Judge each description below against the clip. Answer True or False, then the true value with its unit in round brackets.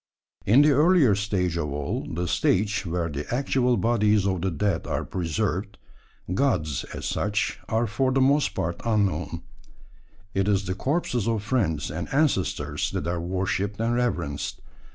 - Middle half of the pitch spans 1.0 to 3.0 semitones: False (5.5 semitones)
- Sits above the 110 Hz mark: False (100 Hz)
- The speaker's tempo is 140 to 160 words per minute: True (155 wpm)